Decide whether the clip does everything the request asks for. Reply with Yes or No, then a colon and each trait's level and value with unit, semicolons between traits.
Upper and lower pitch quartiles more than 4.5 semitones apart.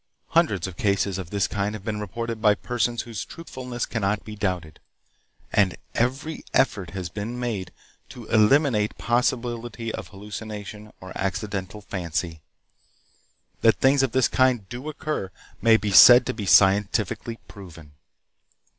No: average, 3.7 semitones